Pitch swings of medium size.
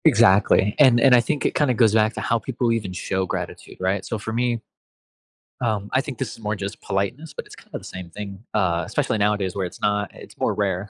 Yes: average, 3.4 semitones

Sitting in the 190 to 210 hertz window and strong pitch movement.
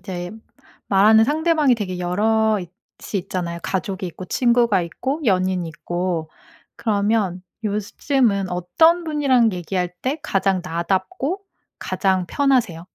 No: high, 195 Hz; average, 5.0 semitones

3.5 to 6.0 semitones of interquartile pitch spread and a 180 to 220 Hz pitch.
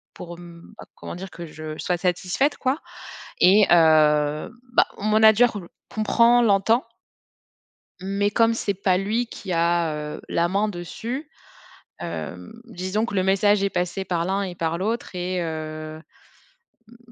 Yes: average, 3.9 semitones; high, 190 Hz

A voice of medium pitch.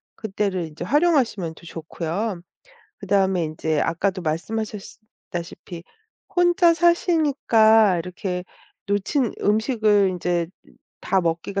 No: high, 200 Hz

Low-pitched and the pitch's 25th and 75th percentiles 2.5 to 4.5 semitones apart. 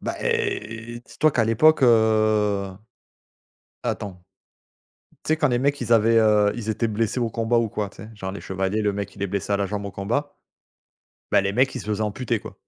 Yes: low, 110 Hz; average, 2.8 semitones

